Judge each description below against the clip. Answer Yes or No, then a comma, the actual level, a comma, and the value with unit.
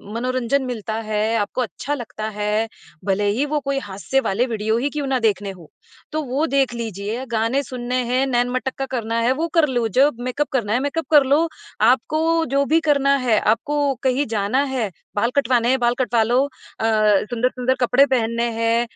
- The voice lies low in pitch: No, very high, 250 Hz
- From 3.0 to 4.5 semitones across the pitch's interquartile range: Yes, average, 3.4 semitones